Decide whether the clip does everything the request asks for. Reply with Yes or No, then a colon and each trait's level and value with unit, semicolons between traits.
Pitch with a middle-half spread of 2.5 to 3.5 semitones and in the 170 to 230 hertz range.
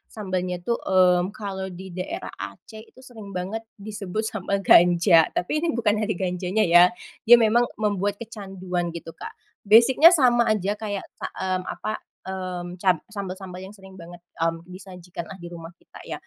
Yes: average, 2.9 semitones; high, 190 Hz